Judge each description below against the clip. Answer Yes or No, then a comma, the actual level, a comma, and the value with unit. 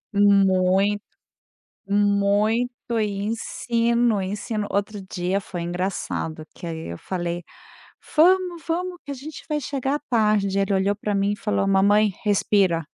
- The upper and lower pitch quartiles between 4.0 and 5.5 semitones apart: No, average, 3.2 semitones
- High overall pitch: Yes, high, 205 Hz